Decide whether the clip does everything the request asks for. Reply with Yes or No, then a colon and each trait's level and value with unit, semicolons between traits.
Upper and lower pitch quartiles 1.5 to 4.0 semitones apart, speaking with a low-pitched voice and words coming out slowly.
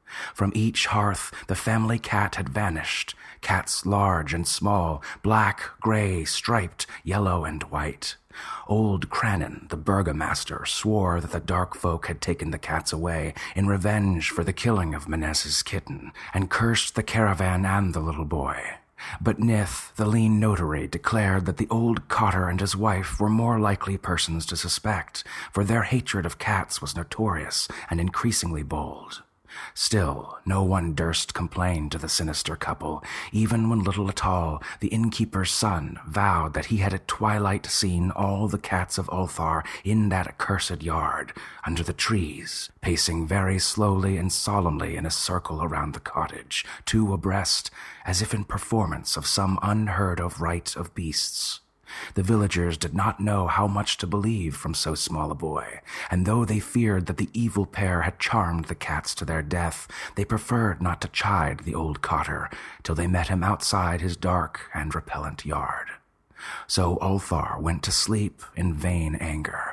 No: average, 3.7 semitones; very low, 95 Hz; average, 165 wpm